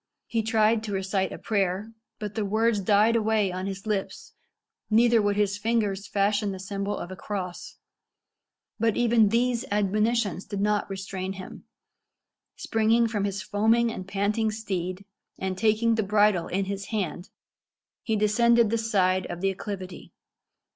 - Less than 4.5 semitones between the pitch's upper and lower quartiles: Yes, narrow, 2.4 semitones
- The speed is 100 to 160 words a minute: Yes, average, 155 wpm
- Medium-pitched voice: No, high, 205 Hz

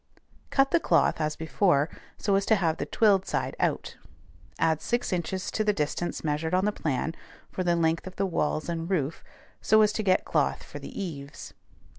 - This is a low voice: No, medium, 175 Hz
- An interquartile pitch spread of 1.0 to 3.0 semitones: No, average, 3.9 semitones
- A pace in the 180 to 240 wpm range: Yes, average, 195 wpm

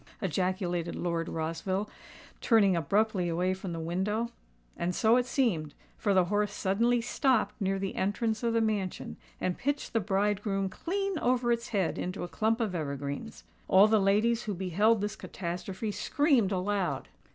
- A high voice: Yes, high, 200 Hz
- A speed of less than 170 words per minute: Yes, average, 160 wpm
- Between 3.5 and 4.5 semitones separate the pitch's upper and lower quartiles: Yes, average, 3.8 semitones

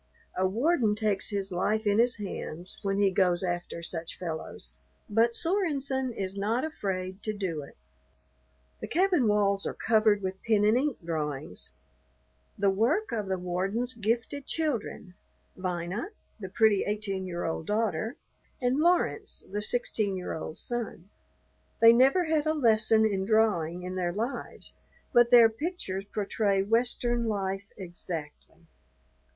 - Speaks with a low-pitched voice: No, high, 210 Hz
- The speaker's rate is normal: Yes, average, 145 wpm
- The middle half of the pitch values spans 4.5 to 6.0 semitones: No, average, 4.0 semitones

